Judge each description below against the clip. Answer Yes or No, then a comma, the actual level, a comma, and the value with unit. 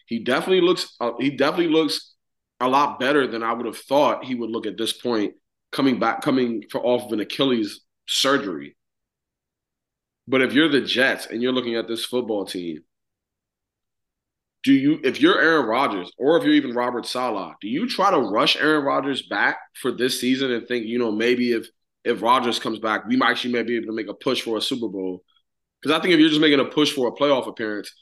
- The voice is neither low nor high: No, low, 125 Hz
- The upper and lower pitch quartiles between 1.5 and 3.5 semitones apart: No, average, 4.8 semitones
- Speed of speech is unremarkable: No, fast, 215 wpm